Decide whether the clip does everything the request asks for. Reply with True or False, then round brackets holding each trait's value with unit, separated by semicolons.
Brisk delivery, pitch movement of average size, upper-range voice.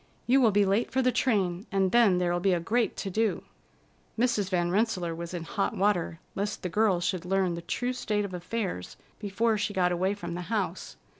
True (210 wpm; 3.5 semitones; 195 Hz)